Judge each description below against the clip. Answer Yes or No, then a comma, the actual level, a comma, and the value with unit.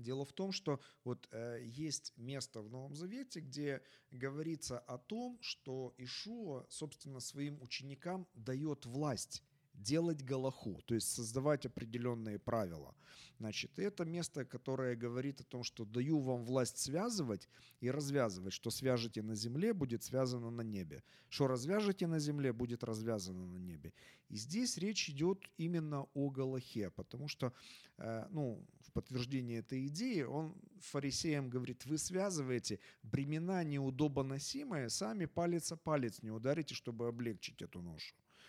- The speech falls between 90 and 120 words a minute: No, average, 140 wpm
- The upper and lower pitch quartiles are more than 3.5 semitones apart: Yes, average, 4.5 semitones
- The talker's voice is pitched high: No, low, 135 Hz